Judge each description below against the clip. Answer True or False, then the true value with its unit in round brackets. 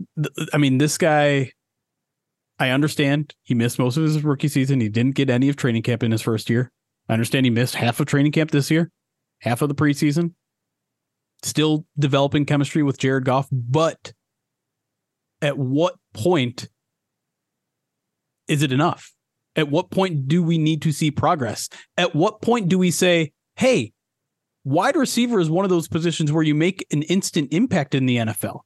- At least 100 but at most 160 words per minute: False (175 wpm)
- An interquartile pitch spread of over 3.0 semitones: True (3.8 semitones)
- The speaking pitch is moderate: True (150 Hz)